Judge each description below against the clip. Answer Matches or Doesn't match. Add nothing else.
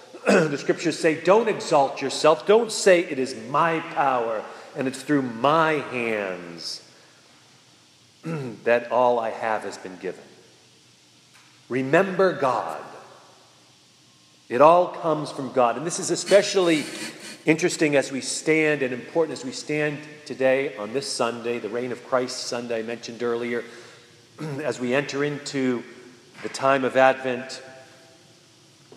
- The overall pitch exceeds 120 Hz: Matches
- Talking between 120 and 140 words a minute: Matches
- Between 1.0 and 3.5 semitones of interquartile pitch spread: Doesn't match